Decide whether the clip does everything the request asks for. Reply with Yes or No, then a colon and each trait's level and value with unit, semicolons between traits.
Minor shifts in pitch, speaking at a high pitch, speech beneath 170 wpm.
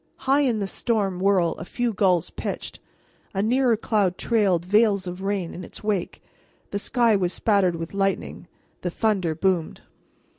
No: average, 3.3 semitones; high, 195 Hz; average, 160 wpm